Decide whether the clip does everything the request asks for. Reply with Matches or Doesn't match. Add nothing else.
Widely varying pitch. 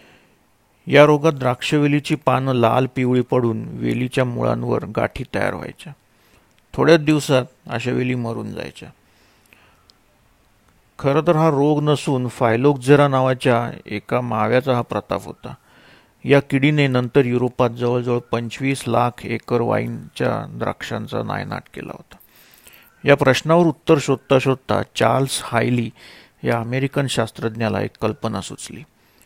Doesn't match